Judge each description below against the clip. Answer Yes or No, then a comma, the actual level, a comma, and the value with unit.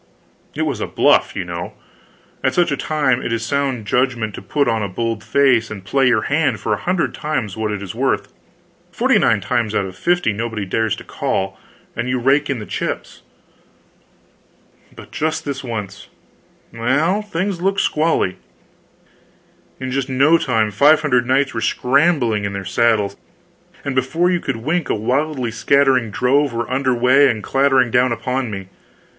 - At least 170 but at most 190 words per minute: Yes, average, 175 wpm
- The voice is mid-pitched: No, low, 125 Hz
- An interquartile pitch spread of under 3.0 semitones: No, average, 4.2 semitones